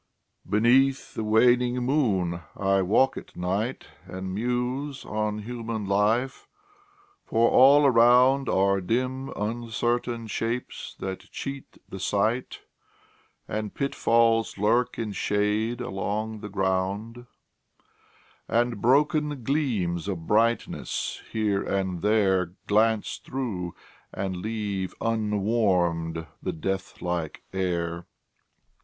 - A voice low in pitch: Yes, low, 110 Hz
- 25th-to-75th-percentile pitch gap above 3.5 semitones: Yes, average, 4.0 semitones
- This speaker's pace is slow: Yes, slow, 100 wpm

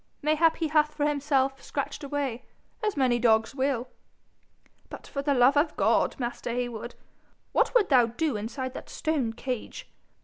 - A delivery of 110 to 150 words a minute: No, average, 165 wpm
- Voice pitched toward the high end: Yes, very high, 270 Hz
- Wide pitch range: No, average, 3.7 semitones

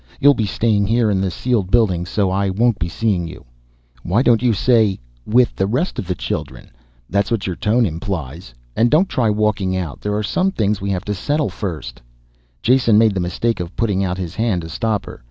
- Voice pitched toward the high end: No, low, 100 Hz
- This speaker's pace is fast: Yes, fast, 220 wpm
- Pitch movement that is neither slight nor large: Yes, average, 4.0 semitones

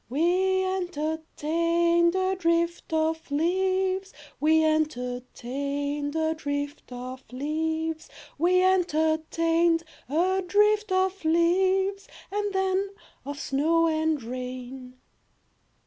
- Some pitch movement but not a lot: Yes, average, 4.2 semitones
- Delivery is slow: Yes, slow, 90 wpm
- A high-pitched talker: Yes, very high, 325 Hz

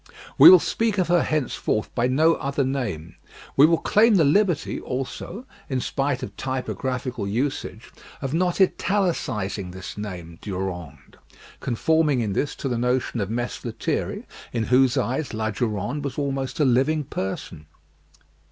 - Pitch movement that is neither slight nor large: No, wide, 5.7 semitones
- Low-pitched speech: Yes, low, 130 Hz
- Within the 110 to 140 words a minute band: No, average, 150 wpm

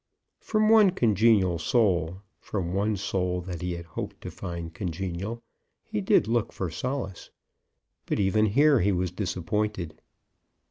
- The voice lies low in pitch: Yes, very low, 95 Hz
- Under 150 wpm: Yes, average, 140 wpm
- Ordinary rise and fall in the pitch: Yes, average, 3.7 semitones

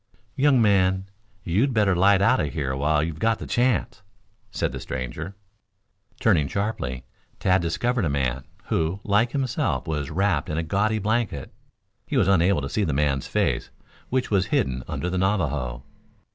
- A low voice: Yes, very low, 95 Hz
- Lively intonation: Yes, wide, 6.3 semitones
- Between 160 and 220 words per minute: Yes, average, 165 wpm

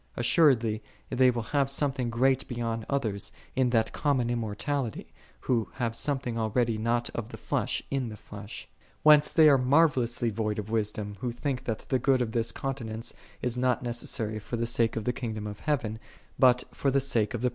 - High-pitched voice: No, low, 120 Hz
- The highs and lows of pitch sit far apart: No, average, 3.0 semitones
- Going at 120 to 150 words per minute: No, average, 200 wpm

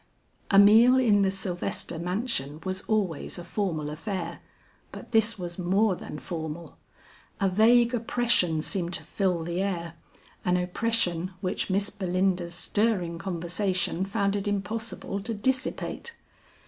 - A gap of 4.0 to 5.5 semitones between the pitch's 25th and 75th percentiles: No, average, 3.4 semitones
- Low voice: No, high, 190 Hz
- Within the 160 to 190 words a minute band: No, slow, 135 wpm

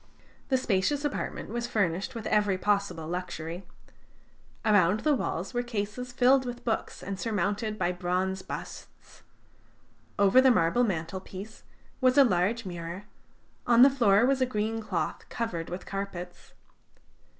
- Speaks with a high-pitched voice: Yes, high, 205 Hz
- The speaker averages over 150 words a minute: No, average, 140 wpm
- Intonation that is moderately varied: Yes, average, 4.7 semitones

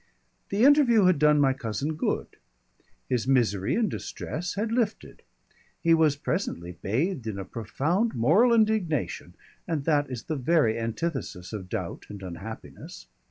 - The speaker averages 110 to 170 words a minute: Yes, average, 145 wpm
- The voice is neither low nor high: Yes, medium, 145 Hz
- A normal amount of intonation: No, wide, 8.5 semitones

